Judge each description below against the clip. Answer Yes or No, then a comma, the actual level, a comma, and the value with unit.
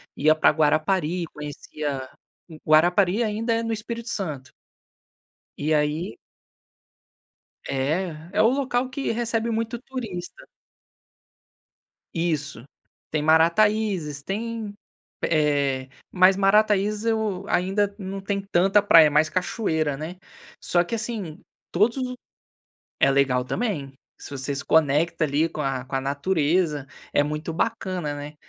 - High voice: No, medium, 175 Hz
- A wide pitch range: Yes, wide, 6.1 semitones